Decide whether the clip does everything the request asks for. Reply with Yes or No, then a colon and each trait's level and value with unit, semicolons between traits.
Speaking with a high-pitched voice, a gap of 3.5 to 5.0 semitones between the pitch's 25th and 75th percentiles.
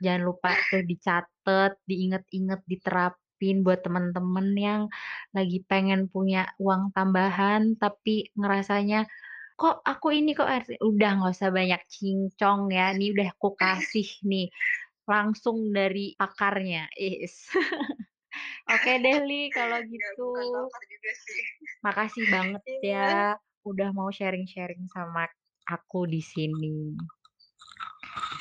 No: high, 195 Hz; narrow, 2.6 semitones